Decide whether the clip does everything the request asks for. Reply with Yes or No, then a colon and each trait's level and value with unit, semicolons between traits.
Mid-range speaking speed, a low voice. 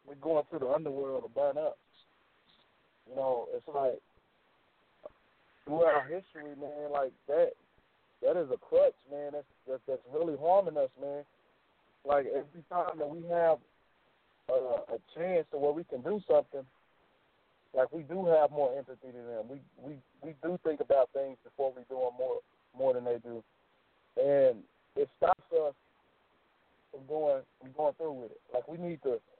No: average, 170 wpm; medium, 160 Hz